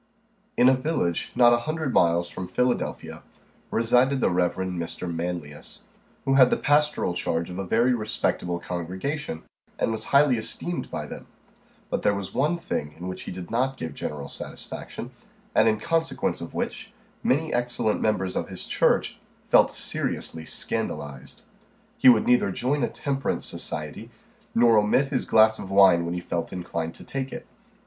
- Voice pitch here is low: Yes, low, 110 Hz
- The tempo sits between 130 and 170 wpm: Yes, average, 165 wpm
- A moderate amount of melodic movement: No, wide, 6.9 semitones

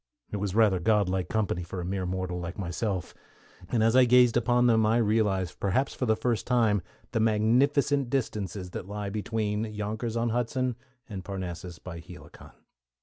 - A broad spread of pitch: No, average, 3.8 semitones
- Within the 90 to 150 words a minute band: No, average, 170 wpm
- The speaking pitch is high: No, low, 105 Hz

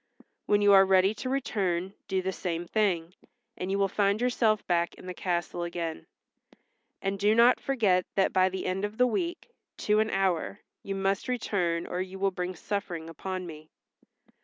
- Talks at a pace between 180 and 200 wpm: Yes, average, 185 wpm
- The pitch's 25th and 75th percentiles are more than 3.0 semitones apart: No, narrow, 2.5 semitones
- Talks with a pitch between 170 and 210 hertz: Yes, high, 190 Hz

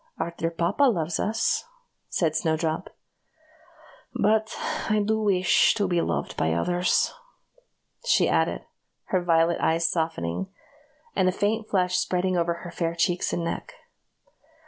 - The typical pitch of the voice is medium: Yes, medium, 175 Hz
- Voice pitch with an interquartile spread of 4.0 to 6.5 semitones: No, average, 3.1 semitones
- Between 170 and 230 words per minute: No, slow, 135 wpm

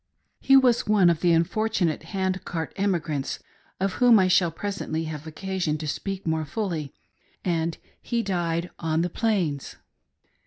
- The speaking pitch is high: No, medium, 175 Hz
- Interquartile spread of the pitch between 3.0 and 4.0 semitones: Yes, average, 3.6 semitones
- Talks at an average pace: Yes, average, 155 wpm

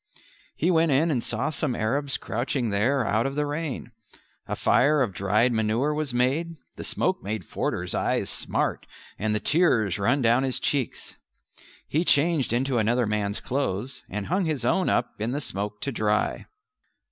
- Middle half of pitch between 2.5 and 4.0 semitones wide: No, average, 5.1 semitones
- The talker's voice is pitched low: Yes, low, 125 Hz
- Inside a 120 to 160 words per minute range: No, average, 170 wpm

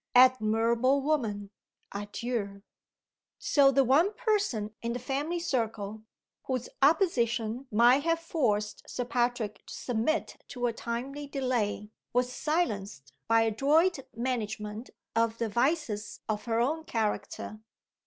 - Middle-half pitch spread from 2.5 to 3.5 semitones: No, average, 4.2 semitones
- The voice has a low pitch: No, high, 240 Hz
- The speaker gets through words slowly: Yes, slow, 120 wpm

